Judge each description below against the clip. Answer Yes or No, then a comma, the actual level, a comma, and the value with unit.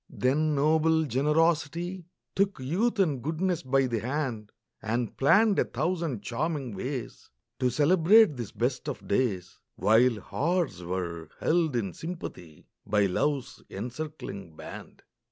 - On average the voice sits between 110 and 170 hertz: Yes, medium, 140 Hz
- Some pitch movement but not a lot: No, wide, 6.1 semitones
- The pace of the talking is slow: Yes, slow, 125 wpm